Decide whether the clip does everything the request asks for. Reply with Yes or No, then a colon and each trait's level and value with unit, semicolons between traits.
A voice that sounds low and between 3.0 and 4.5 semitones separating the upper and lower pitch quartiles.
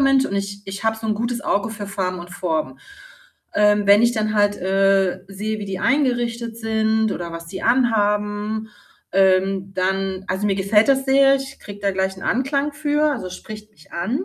No: high, 210 Hz; average, 3.3 semitones